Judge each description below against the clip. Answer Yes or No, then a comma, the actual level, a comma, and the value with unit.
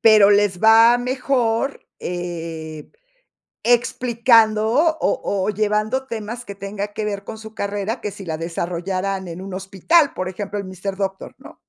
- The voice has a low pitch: No, high, 205 Hz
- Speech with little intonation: No, average, 3.2 semitones